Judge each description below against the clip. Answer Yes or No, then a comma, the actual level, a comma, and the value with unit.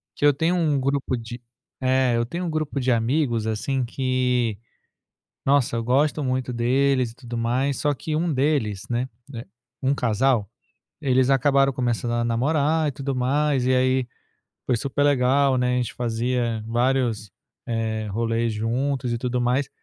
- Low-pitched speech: Yes, low, 130 Hz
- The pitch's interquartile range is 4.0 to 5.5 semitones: No, average, 2.8 semitones